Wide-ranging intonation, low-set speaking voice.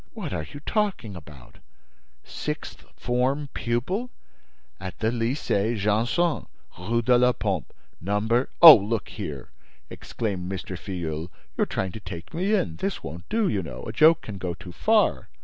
Yes: wide, 5.9 semitones; low, 110 Hz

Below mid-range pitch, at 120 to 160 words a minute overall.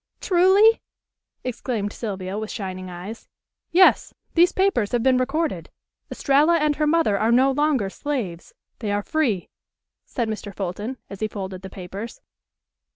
No: high, 230 Hz; average, 145 wpm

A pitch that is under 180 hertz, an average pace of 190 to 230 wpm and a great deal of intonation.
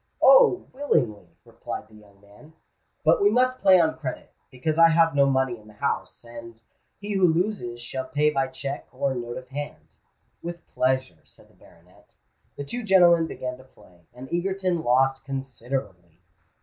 No: low, 135 Hz; average, 170 wpm; wide, 6.1 semitones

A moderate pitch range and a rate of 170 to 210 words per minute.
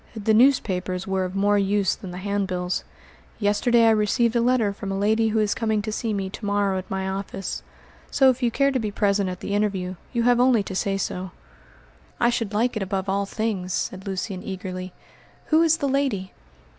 Yes: average, 3.1 semitones; fast, 205 wpm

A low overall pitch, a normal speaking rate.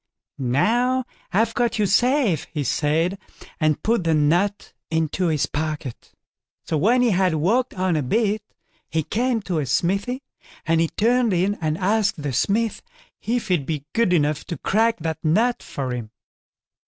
No: medium, 180 Hz; average, 165 wpm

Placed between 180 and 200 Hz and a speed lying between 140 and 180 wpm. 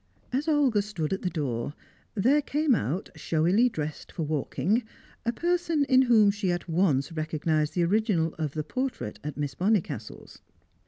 Yes: medium, 185 Hz; average, 160 wpm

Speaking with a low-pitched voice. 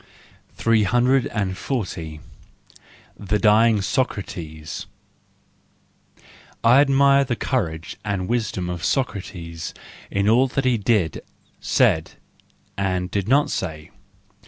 Yes: low, 105 Hz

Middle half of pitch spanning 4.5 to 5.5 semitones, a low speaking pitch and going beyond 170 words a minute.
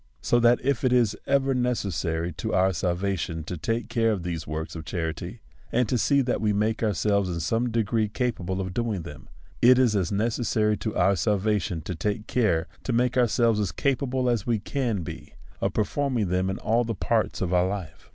Yes: average, 4.8 semitones; low, 105 Hz; fast, 205 wpm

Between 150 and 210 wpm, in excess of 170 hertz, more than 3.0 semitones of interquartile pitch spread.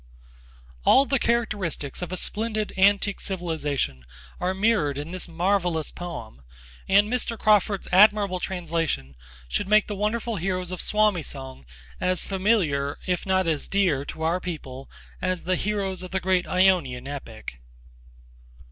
No: average, 140 wpm; medium, 185 Hz; average, 4.2 semitones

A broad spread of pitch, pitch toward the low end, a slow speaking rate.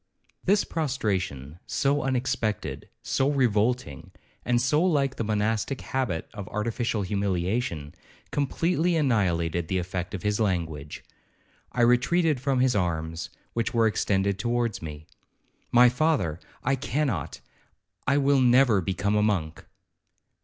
Yes: wide, 6.2 semitones; low, 110 Hz; slow, 120 wpm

